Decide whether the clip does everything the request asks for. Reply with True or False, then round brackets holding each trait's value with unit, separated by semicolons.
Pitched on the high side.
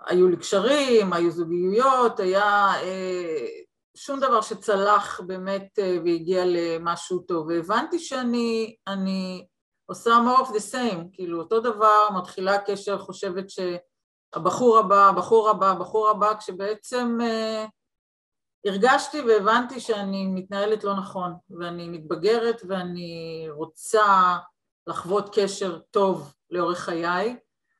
True (200 Hz)